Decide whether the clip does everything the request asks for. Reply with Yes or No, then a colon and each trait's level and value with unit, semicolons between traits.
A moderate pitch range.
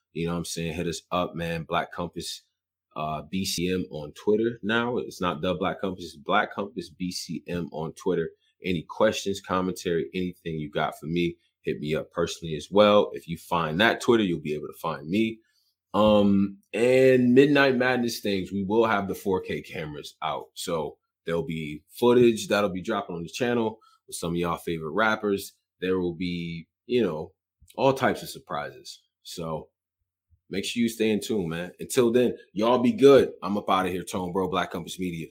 Yes: average, 4.7 semitones